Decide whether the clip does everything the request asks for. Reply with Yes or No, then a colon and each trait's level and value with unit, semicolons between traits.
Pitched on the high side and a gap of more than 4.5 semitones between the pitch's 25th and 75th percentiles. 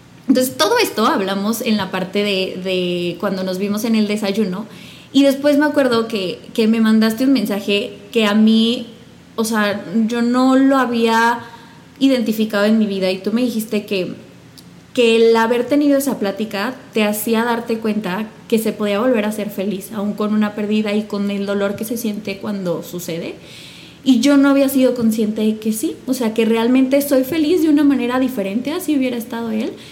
No: high, 225 Hz; average, 3.4 semitones